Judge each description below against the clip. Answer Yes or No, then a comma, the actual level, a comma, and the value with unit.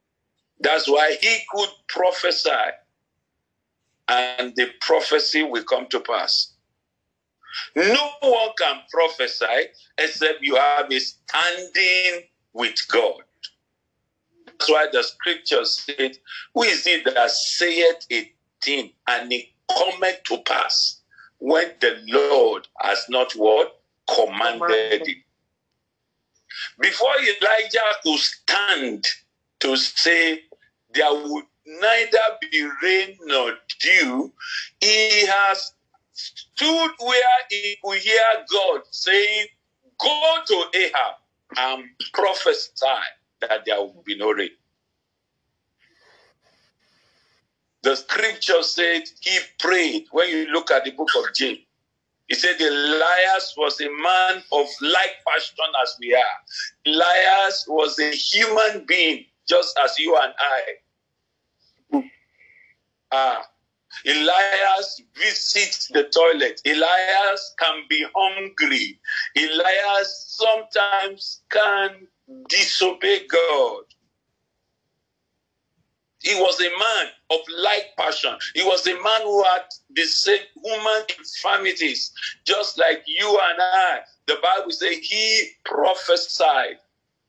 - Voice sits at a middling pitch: No, high, 200 Hz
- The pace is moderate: No, slow, 110 wpm